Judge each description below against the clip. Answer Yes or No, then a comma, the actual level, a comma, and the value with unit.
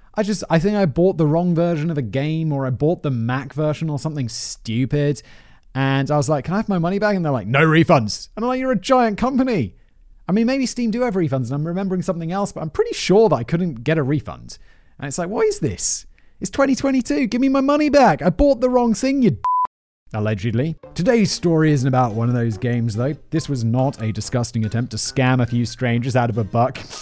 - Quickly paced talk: Yes, fast, 245 wpm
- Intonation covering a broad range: Yes, wide, 8.7 semitones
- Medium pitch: Yes, medium, 155 Hz